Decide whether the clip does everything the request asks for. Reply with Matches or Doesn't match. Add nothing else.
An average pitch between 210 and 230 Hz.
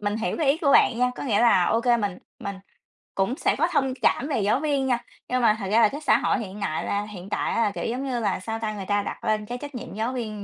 Matches